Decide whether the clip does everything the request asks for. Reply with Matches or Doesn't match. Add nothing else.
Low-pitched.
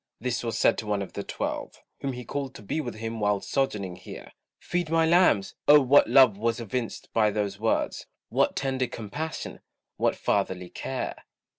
Matches